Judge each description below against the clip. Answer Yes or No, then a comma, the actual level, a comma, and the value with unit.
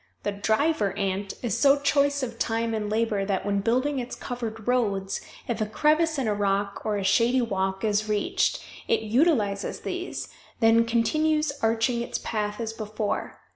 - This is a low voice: No, high, 225 Hz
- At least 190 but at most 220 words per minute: No, average, 170 wpm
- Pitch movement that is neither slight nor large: Yes, average, 3.4 semitones